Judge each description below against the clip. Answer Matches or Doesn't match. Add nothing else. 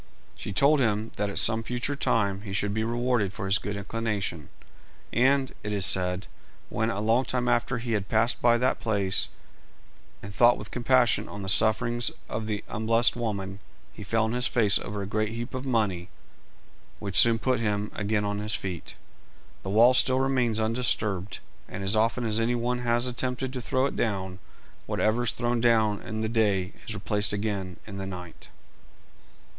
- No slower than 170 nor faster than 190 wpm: Matches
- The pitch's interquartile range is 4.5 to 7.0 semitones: Doesn't match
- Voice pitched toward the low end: Matches